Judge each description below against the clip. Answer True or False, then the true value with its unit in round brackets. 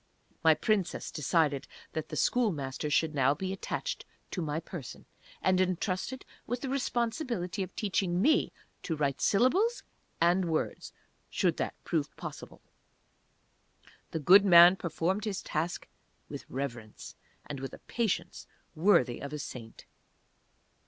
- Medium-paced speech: False (130 wpm)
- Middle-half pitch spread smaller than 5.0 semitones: False (5.3 semitones)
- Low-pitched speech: False (175 Hz)